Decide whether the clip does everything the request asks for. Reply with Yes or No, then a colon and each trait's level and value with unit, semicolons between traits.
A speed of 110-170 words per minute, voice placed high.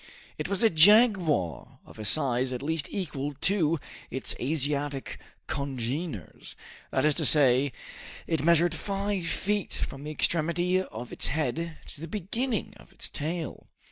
No: average, 145 wpm; medium, 155 Hz